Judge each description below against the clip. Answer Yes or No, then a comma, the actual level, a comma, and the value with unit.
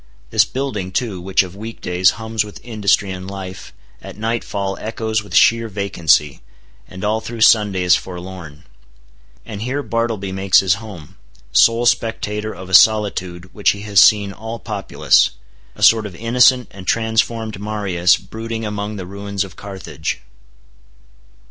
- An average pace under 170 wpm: Yes, average, 150 wpm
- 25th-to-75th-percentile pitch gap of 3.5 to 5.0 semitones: No, average, 3.0 semitones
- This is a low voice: Yes, low, 100 Hz